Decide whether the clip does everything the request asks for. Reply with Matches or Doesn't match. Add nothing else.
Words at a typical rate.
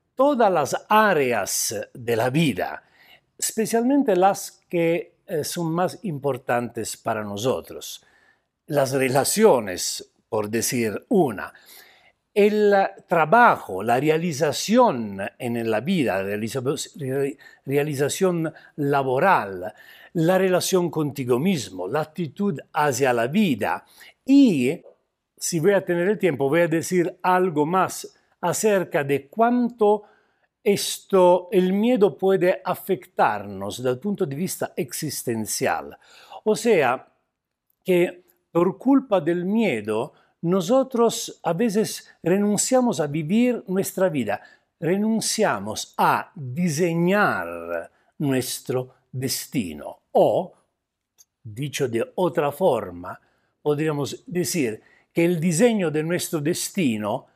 Doesn't match